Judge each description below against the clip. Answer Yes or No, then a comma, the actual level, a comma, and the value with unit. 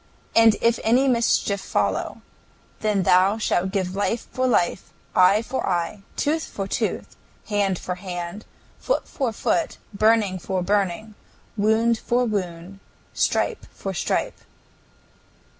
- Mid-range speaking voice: No, high, 205 Hz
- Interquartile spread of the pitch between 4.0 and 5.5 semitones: No, average, 3.5 semitones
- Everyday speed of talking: No, slow, 125 wpm